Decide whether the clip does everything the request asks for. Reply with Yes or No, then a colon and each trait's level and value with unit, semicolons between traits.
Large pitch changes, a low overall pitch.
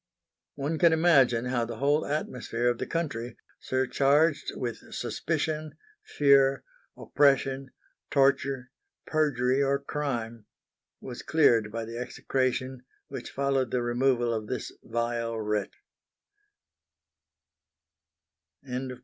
No: average, 2.8 semitones; low, 130 Hz